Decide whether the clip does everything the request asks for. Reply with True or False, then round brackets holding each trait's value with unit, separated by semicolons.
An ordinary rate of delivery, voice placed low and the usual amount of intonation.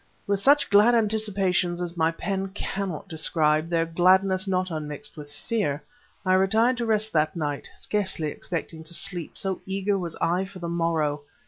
False (165 wpm; 185 Hz; 3.5 semitones)